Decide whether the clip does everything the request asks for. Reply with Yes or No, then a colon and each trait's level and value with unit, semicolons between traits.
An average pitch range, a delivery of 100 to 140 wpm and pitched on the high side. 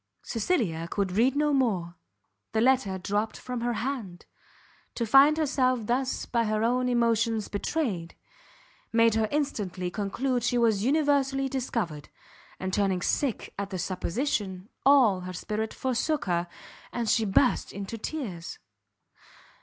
Yes: average, 5.0 semitones; slow, 135 wpm; high, 230 Hz